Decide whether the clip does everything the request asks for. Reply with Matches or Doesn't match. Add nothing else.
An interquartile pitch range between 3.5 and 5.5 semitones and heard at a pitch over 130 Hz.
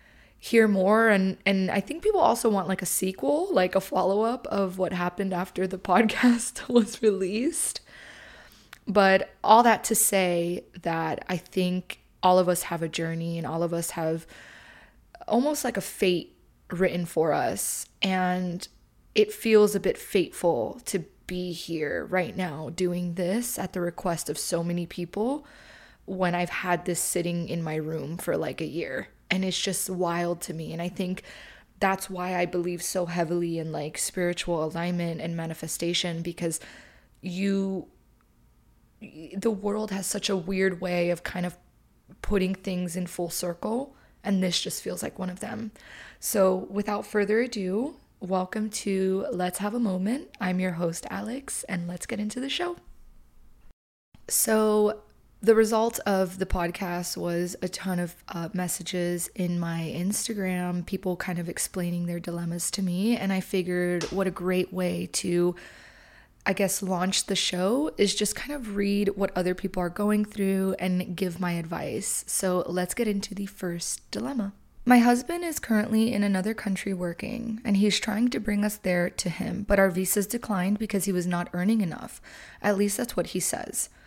Doesn't match